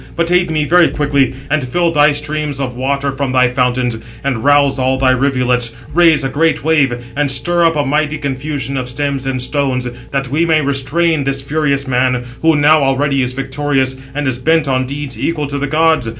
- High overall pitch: No, medium, 140 Hz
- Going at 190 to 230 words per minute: Yes, average, 200 wpm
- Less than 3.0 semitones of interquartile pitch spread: Yes, narrow, 2.6 semitones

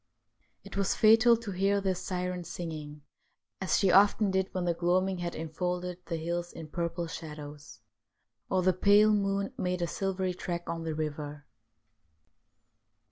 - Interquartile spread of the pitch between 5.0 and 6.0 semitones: No, average, 2.7 semitones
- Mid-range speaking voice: Yes, medium, 180 Hz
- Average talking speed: Yes, average, 155 wpm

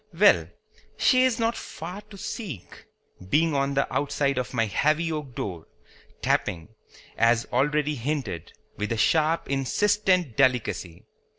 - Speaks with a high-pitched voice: No, medium, 140 Hz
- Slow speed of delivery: Yes, slow, 130 wpm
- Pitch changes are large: Yes, wide, 5.8 semitones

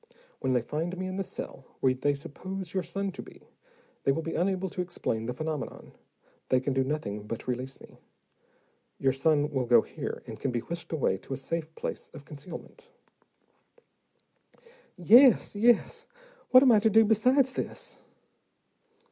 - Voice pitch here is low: No, medium, 160 Hz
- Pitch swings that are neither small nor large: No, wide, 6.4 semitones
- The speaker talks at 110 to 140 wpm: No, average, 170 wpm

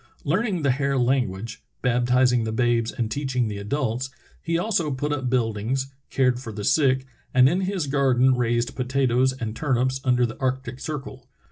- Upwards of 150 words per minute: Yes, average, 165 wpm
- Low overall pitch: Yes, low, 130 Hz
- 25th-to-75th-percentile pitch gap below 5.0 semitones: Yes, narrow, 2.4 semitones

